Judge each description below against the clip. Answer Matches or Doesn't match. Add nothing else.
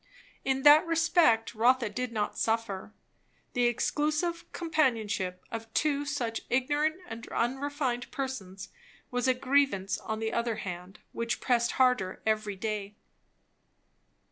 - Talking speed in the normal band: Doesn't match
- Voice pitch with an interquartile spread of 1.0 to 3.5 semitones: Doesn't match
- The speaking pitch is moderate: Doesn't match